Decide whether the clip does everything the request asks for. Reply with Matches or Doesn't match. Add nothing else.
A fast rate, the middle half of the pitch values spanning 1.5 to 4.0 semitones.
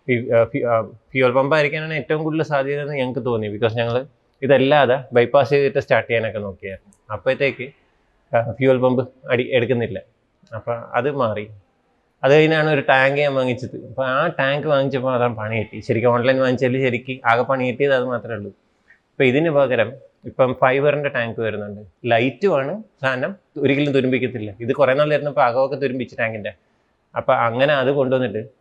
Matches